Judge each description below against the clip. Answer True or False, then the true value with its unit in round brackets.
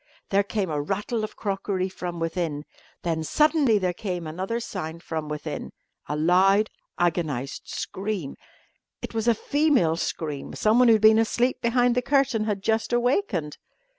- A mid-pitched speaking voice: False (195 Hz)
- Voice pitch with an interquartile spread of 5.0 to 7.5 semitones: True (5.6 semitones)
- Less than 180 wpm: True (155 wpm)